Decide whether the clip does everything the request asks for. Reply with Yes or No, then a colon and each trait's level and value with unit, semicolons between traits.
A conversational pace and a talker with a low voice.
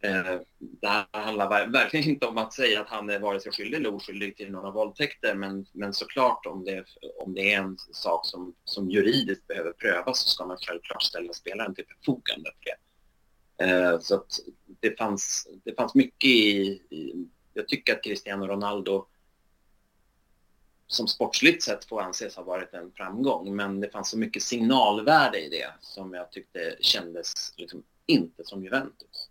Yes: average, 165 wpm; low, 100 Hz